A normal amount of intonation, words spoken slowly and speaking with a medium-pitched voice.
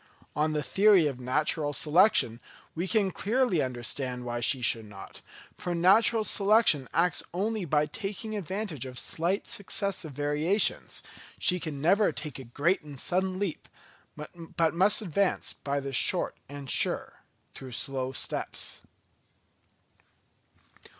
No: wide, 6.2 semitones; slow, 130 wpm; medium, 160 Hz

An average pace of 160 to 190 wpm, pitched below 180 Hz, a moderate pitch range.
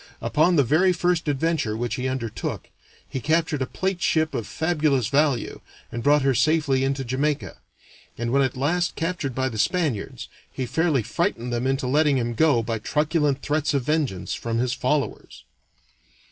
Yes: average, 170 wpm; medium, 140 Hz; average, 3.9 semitones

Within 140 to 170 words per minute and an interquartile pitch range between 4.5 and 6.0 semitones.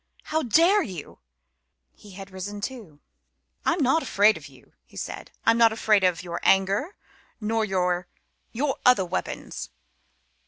Yes: average, 150 wpm; average, 5.2 semitones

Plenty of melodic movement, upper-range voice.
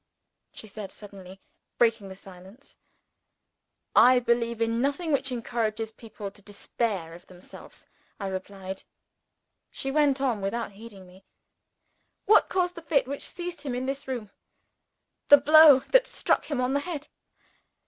Yes: wide, 5.9 semitones; high, 235 Hz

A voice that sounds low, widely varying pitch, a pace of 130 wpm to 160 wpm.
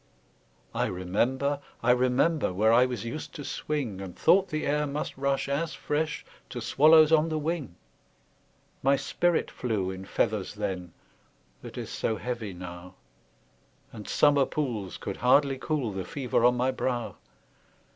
Yes: low, 125 Hz; wide, 6.0 semitones; average, 150 wpm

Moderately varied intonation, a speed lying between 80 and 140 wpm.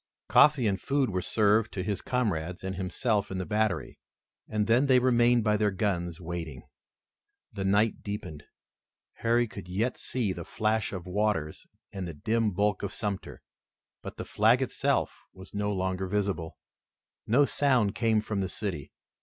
No: average, 3.4 semitones; average, 160 wpm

